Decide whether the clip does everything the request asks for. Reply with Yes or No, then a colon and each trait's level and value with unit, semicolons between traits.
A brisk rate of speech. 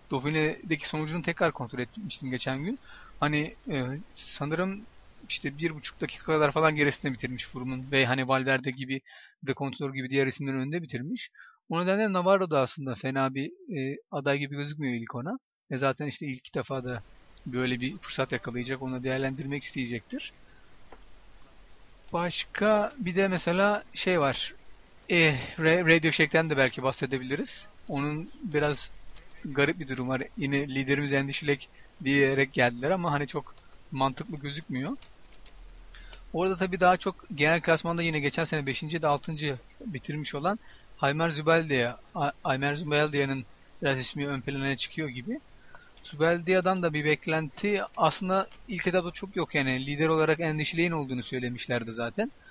Yes: fast, 145 wpm